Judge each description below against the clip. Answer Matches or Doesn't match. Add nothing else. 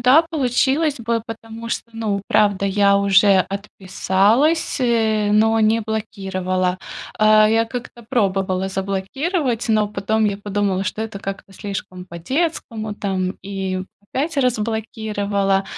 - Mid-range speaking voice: Doesn't match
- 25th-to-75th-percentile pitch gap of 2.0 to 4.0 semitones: Matches